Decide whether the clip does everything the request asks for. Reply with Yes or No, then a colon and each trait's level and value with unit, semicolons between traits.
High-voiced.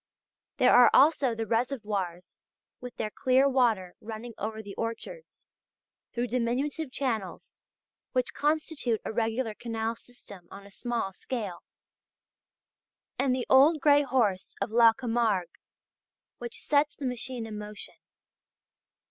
Yes: high, 235 Hz